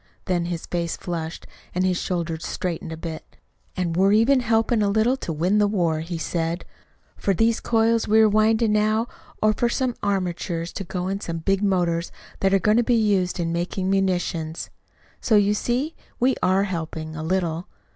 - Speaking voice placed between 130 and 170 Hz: No, high, 190 Hz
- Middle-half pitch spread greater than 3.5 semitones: Yes, average, 4.1 semitones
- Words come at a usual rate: Yes, average, 185 wpm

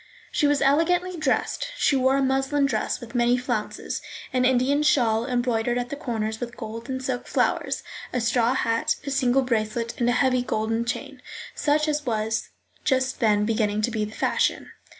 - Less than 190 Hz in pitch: No, high, 245 Hz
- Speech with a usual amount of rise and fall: Yes, average, 3.0 semitones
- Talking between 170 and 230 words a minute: Yes, average, 180 wpm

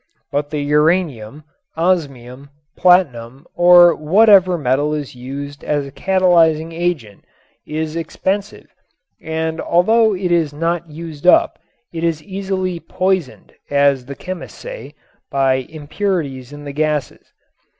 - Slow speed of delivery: Yes, slow, 120 wpm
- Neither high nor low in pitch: Yes, medium, 160 Hz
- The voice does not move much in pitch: No, average, 3.9 semitones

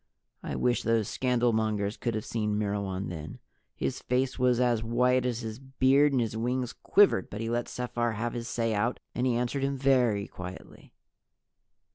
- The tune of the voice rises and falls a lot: No, average, 2.7 semitones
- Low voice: Yes, low, 120 Hz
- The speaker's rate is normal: Yes, average, 175 wpm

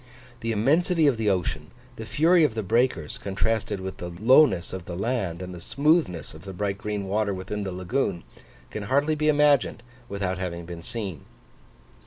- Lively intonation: Yes, wide, 6.0 semitones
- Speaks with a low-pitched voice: Yes, low, 105 Hz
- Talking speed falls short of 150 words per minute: No, average, 180 wpm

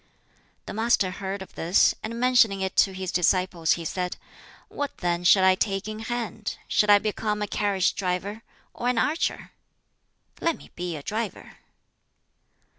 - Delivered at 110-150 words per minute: No, average, 160 wpm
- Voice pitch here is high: Yes, high, 200 Hz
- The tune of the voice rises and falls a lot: No, average, 3.4 semitones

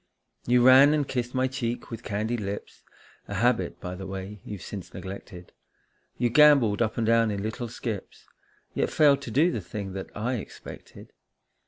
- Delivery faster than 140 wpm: Yes, average, 175 wpm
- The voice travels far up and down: No, average, 4.0 semitones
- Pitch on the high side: No, low, 115 Hz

